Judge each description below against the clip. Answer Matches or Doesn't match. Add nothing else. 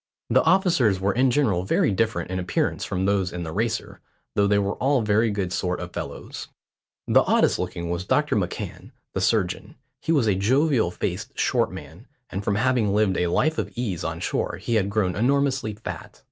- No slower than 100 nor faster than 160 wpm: Doesn't match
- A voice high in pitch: Doesn't match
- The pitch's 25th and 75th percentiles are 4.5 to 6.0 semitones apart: Matches